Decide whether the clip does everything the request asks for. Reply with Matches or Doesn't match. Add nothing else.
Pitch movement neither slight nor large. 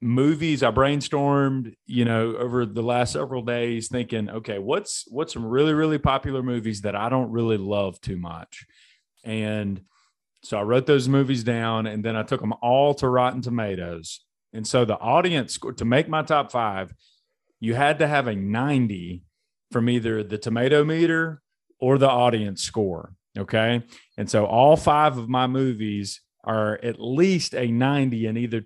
Matches